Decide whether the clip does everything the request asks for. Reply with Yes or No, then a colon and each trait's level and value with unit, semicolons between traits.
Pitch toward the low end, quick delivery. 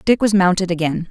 No: medium, 185 Hz; fast, 215 wpm